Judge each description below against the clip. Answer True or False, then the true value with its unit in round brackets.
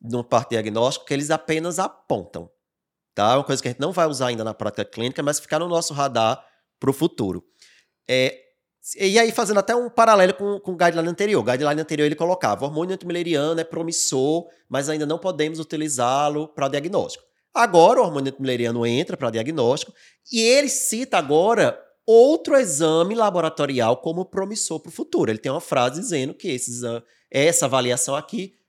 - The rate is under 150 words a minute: False (180 wpm)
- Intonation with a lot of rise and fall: True (6.3 semitones)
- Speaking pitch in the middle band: True (160 Hz)